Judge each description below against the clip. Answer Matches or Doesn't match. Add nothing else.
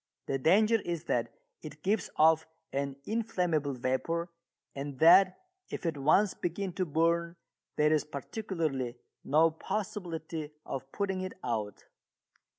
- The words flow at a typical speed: Doesn't match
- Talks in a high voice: Doesn't match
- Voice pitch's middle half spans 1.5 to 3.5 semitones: Doesn't match